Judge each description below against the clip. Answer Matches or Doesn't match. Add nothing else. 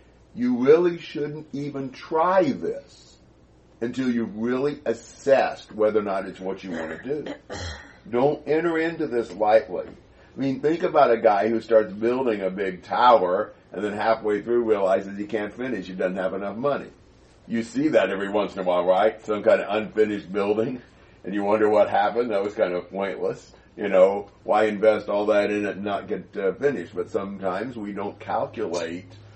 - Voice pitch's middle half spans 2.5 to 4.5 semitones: Matches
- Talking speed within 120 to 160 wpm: Doesn't match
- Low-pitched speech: Matches